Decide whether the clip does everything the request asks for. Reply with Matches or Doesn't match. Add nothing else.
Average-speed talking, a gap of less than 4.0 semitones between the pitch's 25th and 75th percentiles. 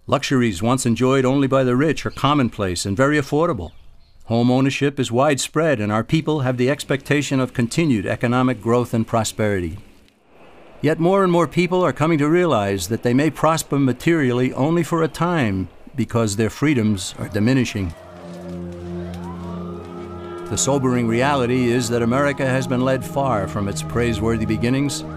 Doesn't match